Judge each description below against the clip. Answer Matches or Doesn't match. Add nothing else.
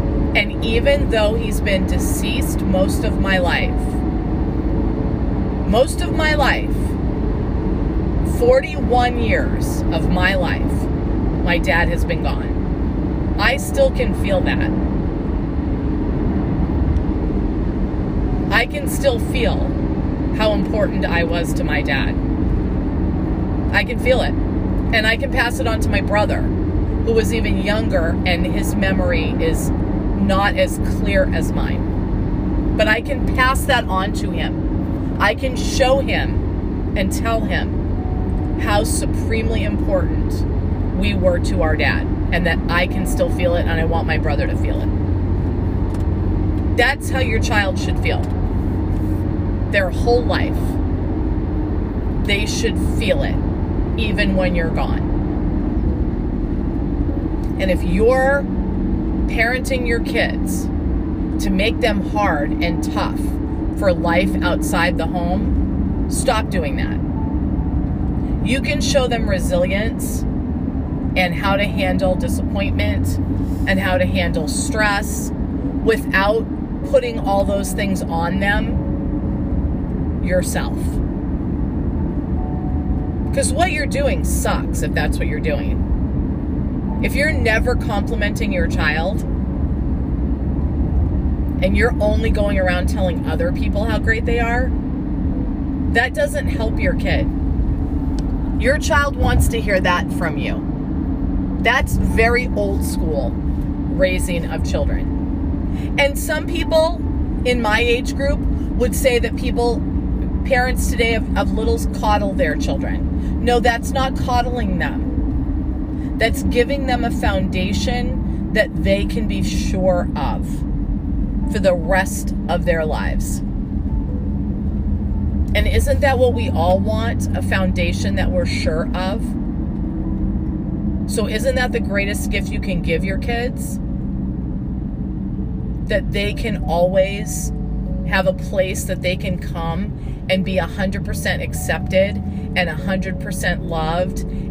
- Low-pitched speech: Matches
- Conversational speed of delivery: Doesn't match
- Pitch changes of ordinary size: Matches